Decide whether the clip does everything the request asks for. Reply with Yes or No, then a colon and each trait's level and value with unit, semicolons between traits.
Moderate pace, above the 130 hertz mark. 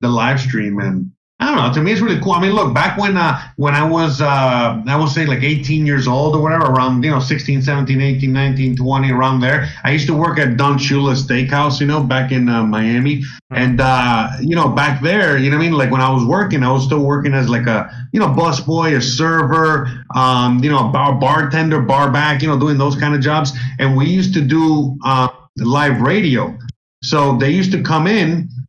No: fast, 235 wpm; medium, 140 Hz